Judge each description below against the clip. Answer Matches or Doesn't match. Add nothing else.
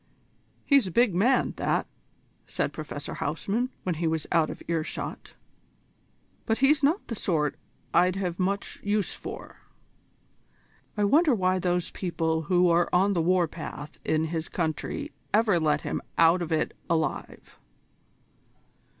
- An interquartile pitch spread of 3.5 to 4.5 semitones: Matches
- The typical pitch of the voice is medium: Matches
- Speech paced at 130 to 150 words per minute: Matches